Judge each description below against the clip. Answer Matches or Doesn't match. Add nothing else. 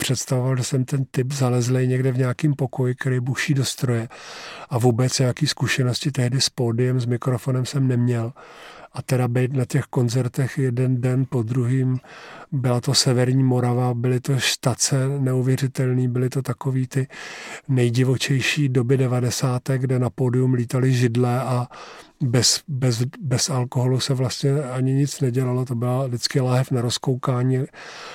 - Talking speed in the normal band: Matches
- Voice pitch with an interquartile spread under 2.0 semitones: Matches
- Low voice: Matches